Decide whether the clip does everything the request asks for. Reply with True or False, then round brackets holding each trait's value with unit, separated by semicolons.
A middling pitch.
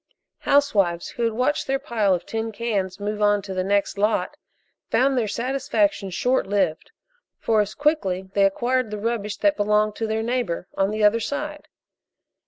False (215 Hz)